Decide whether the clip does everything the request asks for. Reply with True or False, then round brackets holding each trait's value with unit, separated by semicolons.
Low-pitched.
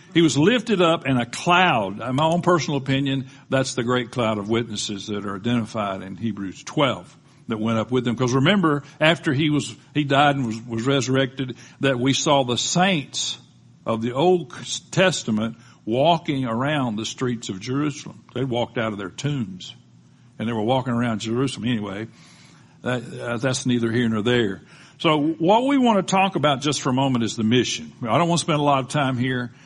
True (130 Hz)